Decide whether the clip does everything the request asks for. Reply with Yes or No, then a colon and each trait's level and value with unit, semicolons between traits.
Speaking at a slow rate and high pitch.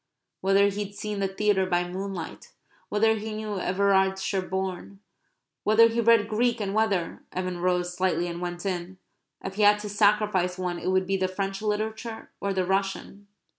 No: average, 170 wpm; high, 195 Hz